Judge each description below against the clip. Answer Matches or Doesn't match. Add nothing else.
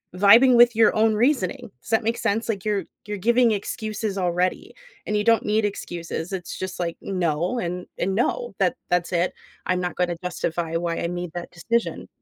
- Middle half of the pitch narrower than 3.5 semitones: Doesn't match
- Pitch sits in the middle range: Doesn't match